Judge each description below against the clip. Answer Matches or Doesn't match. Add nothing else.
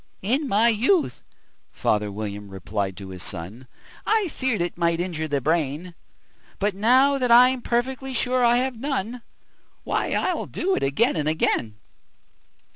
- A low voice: Doesn't match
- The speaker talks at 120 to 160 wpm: Matches